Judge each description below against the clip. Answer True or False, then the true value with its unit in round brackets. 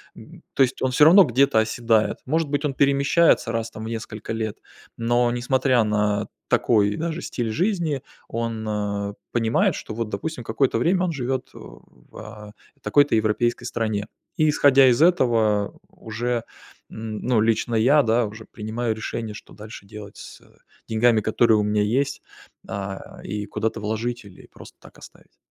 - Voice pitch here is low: True (115 Hz)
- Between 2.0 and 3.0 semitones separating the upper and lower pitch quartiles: False (3.4 semitones)